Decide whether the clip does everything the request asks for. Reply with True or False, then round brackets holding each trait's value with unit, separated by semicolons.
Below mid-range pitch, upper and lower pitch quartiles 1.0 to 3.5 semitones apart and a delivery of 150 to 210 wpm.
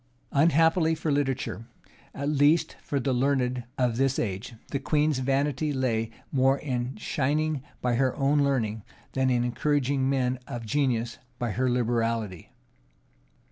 False (130 Hz; 2.9 semitones; 140 wpm)